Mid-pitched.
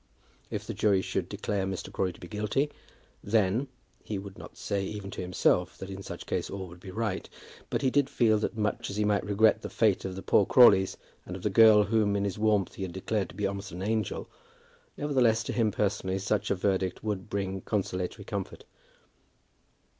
No: low, 100 Hz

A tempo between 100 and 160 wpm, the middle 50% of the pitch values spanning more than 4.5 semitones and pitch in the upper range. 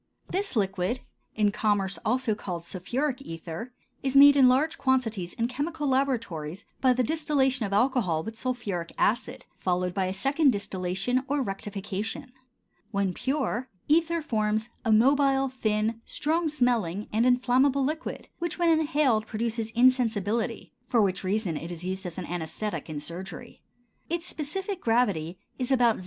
Yes: average, 150 wpm; wide, 5.6 semitones; high, 235 Hz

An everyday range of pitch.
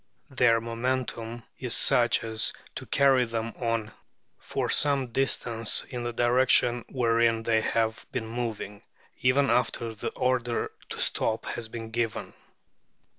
No: narrow, 1.7 semitones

